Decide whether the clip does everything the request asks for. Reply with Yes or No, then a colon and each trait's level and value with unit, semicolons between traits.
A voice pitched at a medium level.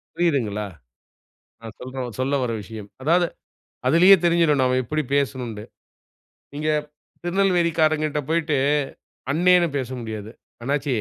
Yes: medium, 145 Hz